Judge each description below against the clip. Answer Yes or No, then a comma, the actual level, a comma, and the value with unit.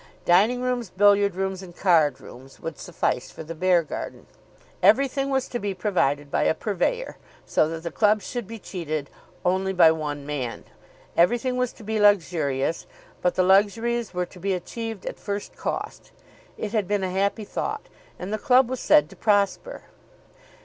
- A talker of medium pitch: No, high, 195 Hz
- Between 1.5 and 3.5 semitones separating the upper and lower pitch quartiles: No, average, 4.9 semitones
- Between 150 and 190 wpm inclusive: Yes, average, 170 wpm